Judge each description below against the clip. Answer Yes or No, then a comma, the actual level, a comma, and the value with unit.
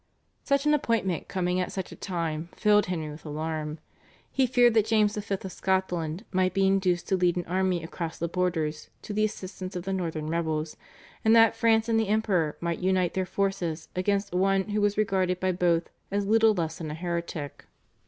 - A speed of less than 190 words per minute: No, average, 195 wpm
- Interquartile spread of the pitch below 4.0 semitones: Yes, average, 3.4 semitones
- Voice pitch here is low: No, medium, 185 Hz